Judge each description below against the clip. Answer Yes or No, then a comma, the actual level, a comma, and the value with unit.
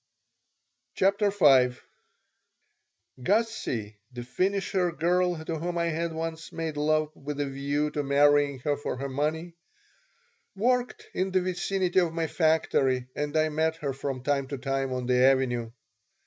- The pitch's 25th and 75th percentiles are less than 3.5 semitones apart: No, average, 4.1 semitones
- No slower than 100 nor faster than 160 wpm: Yes, average, 150 wpm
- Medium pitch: Yes, medium, 150 Hz